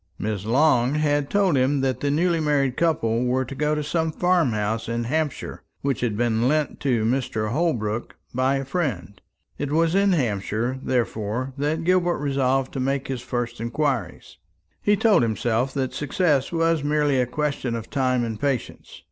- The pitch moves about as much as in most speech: Yes, average, 4.2 semitones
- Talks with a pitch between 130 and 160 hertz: Yes, low, 135 Hz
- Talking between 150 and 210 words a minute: Yes, average, 175 wpm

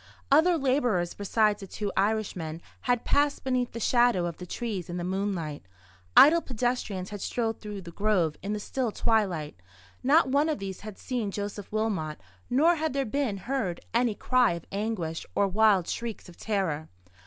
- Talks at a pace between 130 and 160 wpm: No, average, 175 wpm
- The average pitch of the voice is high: Yes, high, 210 Hz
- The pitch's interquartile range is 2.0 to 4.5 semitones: No, average, 5.0 semitones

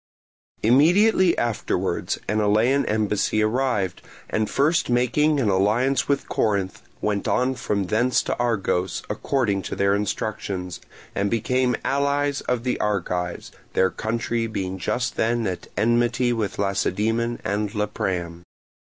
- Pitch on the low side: Yes, low, 110 Hz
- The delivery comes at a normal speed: No, slow, 125 wpm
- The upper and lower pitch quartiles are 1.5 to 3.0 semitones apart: No, average, 3.9 semitones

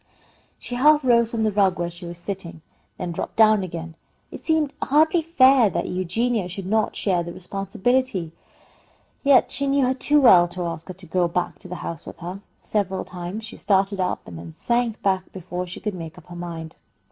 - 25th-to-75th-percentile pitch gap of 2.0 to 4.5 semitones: No, average, 5.3 semitones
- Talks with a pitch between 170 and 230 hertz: Yes, high, 190 Hz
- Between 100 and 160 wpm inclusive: No, fast, 205 wpm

